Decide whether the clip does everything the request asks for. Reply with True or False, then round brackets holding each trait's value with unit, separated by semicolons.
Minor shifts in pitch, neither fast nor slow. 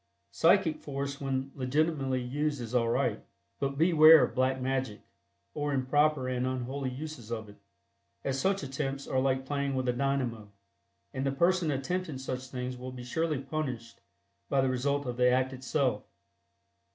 True (2.2 semitones; 165 wpm)